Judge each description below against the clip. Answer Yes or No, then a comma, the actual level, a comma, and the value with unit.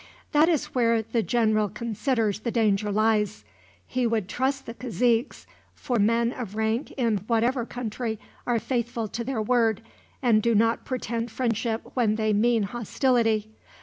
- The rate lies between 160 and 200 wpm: No, average, 150 wpm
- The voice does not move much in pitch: Yes, narrow, 2.0 semitones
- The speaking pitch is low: No, high, 230 Hz